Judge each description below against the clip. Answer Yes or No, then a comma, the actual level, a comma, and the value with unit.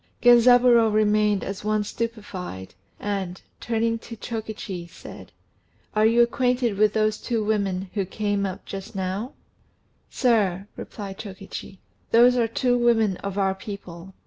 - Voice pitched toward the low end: No, high, 210 Hz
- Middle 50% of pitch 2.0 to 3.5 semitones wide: Yes, average, 3.0 semitones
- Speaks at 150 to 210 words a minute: No, slow, 135 wpm